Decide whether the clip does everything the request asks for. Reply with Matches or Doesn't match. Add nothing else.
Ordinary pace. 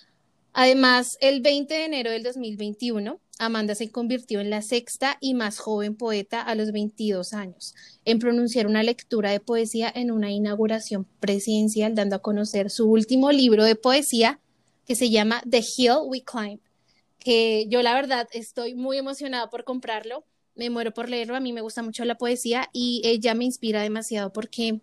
Matches